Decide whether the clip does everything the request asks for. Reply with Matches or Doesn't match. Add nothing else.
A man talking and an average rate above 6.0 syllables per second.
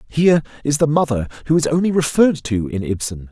Matches